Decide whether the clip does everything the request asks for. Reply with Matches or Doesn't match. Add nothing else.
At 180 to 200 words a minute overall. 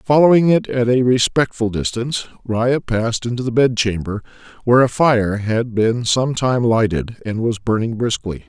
Doesn't match